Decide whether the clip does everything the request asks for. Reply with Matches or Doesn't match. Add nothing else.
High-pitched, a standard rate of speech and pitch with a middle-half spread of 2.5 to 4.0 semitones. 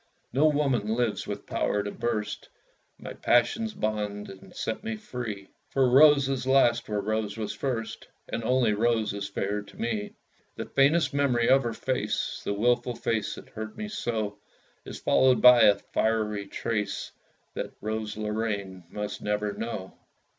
Doesn't match